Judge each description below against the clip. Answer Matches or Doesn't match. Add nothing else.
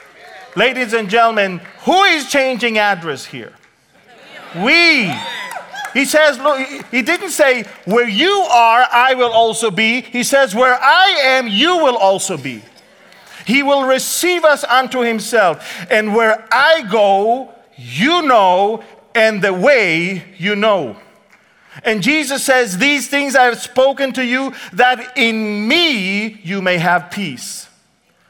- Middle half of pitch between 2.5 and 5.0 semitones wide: Matches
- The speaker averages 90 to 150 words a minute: Matches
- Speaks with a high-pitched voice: Matches